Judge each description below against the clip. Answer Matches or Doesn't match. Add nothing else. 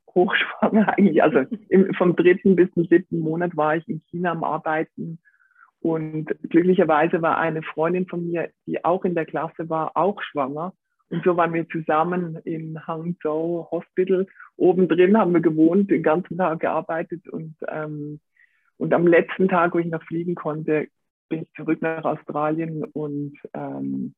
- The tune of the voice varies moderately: Doesn't match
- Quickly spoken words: Doesn't match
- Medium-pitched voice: Matches